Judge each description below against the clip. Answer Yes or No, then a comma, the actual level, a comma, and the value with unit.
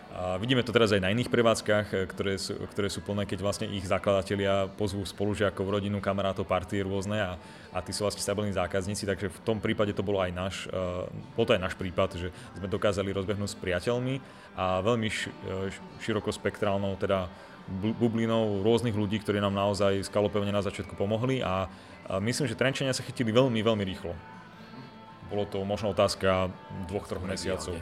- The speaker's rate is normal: No, fast, 170 wpm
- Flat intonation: Yes, narrow, 1.8 semitones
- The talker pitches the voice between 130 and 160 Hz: No, low, 100 Hz